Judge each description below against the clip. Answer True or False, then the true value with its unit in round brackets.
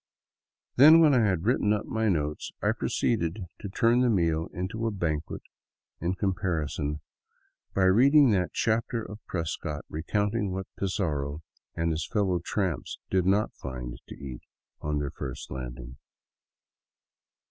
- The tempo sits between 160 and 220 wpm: False (140 wpm)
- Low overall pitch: True (95 Hz)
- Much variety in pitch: True (6.0 semitones)